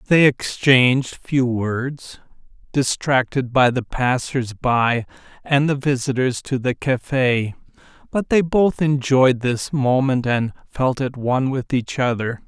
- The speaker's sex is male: Yes, male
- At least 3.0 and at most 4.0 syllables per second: Yes, 3.8 syllables/s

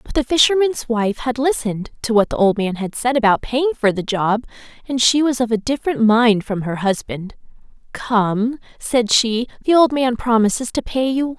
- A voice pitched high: Yes, high, 240 Hz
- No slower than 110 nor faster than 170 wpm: No, fast, 205 wpm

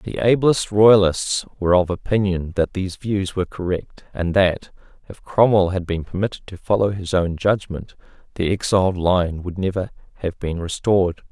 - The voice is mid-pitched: No, very low, 95 Hz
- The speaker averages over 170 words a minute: No, average, 165 wpm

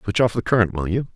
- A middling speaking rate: No, fast, 310 wpm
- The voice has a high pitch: No, low, 105 Hz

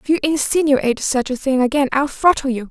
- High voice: Yes, very high, 275 Hz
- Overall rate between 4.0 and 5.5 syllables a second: No, 6.0 syllables/s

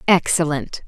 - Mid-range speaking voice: Yes, medium, 160 Hz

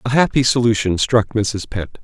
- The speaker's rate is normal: Yes, average, 175 wpm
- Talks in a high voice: No, low, 115 Hz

